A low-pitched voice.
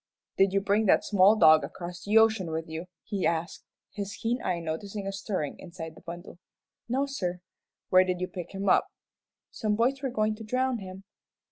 No: high, 195 Hz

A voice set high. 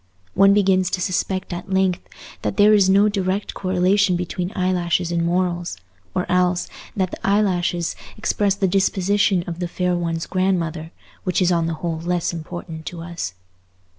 No: medium, 180 Hz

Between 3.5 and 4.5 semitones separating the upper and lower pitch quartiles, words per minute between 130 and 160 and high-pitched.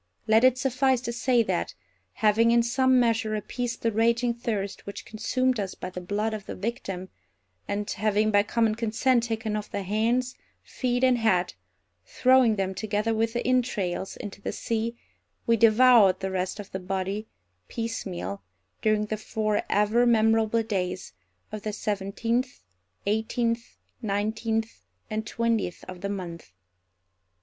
No: narrow, 2.6 semitones; average, 150 wpm; high, 220 Hz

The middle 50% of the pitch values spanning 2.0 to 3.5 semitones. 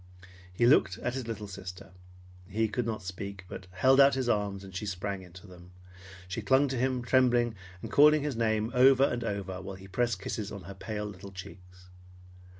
No: average, 4.3 semitones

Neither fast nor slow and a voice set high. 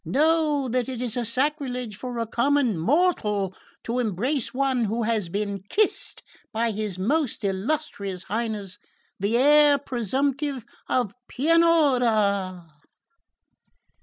No: slow, 110 wpm; high, 240 Hz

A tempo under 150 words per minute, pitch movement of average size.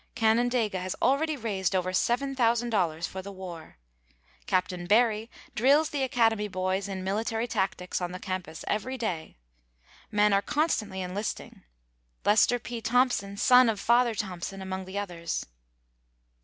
Yes: slow, 135 wpm; average, 4.2 semitones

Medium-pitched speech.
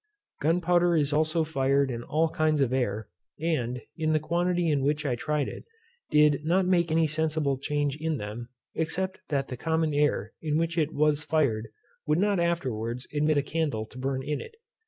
Yes: medium, 150 Hz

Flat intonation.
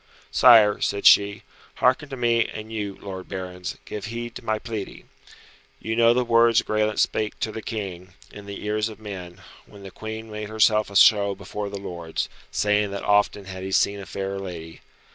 Yes: narrow, 2.0 semitones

